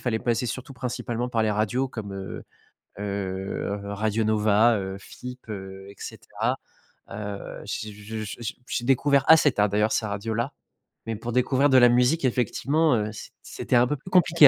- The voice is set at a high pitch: No, low, 115 Hz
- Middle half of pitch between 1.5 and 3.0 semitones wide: No, average, 3.5 semitones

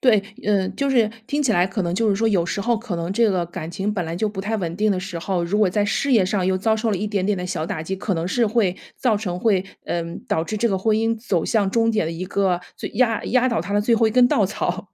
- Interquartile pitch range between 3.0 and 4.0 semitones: Yes, average, 3.5 semitones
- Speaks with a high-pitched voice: Yes, high, 200 Hz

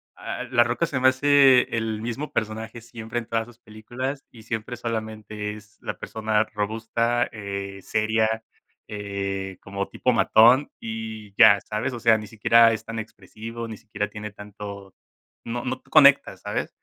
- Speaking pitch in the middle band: No, low, 110 Hz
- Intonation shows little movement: Yes, narrow, 2.0 semitones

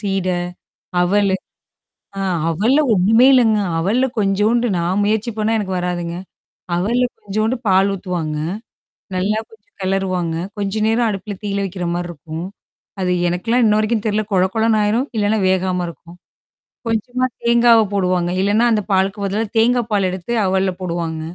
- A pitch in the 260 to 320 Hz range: No, high, 200 Hz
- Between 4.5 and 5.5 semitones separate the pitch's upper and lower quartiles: No, average, 3.3 semitones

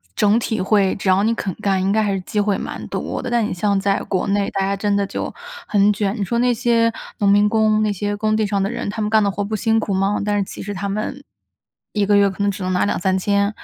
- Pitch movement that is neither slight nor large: No, narrow, 1.5 semitones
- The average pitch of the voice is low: No, high, 205 Hz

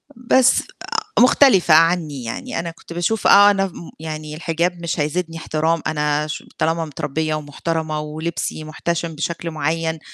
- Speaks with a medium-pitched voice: Yes, medium, 165 Hz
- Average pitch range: No, narrow, 2.0 semitones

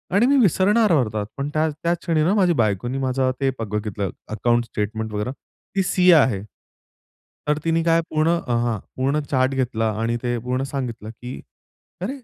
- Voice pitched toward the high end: No, low, 130 Hz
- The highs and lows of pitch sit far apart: Yes, wide, 6.4 semitones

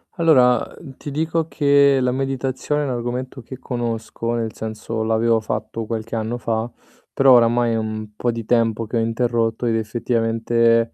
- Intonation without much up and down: Yes, narrow, 2.3 semitones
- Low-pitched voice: Yes, low, 115 Hz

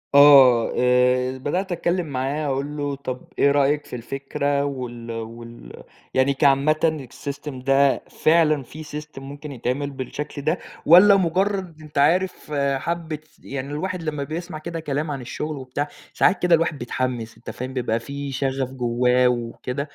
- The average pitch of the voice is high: No, medium, 140 Hz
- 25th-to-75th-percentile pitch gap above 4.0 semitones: No, average, 3.2 semitones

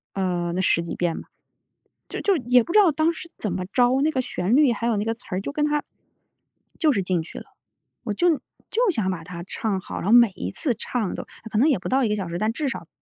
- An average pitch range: No, wide, 7.2 semitones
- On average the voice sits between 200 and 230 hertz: Yes, high, 225 Hz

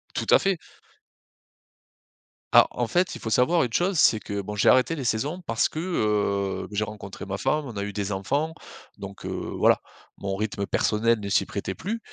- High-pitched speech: No, low, 110 Hz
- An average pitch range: No, wide, 7.2 semitones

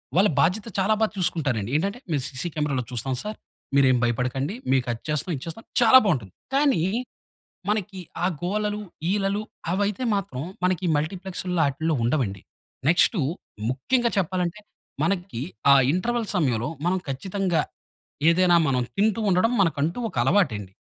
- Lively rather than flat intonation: Yes, wide, 6.8 semitones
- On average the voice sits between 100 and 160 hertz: No, medium, 175 Hz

